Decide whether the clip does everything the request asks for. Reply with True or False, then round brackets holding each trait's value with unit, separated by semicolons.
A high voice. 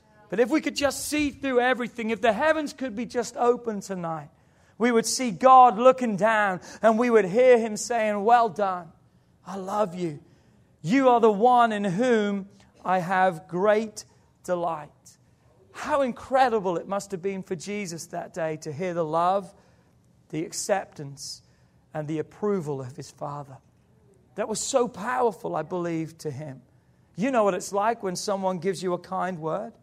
True (200 Hz)